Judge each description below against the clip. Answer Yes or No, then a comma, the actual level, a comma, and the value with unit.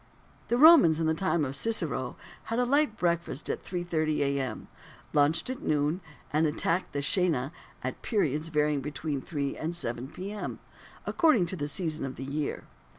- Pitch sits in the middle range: Yes, medium, 160 Hz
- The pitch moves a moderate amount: Yes, average, 4.0 semitones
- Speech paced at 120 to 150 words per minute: No, average, 165 wpm